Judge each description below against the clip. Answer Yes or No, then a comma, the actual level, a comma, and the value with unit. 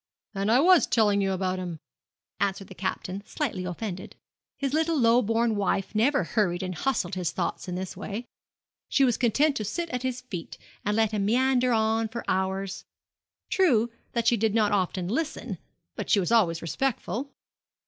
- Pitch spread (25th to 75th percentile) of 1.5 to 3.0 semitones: No, average, 4.7 semitones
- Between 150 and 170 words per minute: No, average, 180 wpm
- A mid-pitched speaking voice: No, high, 215 Hz